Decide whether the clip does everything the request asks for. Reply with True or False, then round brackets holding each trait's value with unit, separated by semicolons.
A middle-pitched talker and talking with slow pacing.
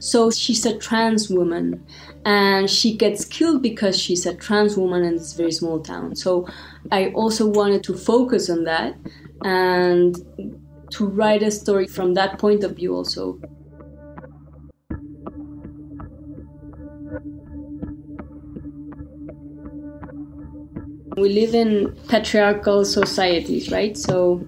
True (180 Hz; 110 wpm)